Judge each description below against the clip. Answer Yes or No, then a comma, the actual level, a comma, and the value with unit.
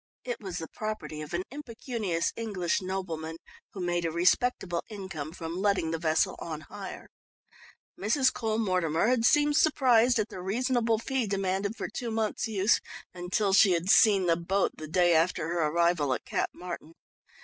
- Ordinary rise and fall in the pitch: Yes, average, 4.8 semitones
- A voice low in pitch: No, high, 190 Hz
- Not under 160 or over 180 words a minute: Yes, average, 170 wpm